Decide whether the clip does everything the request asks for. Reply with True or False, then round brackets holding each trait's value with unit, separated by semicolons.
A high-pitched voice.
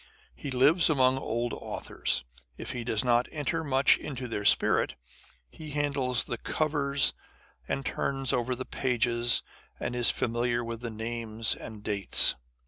False (125 Hz)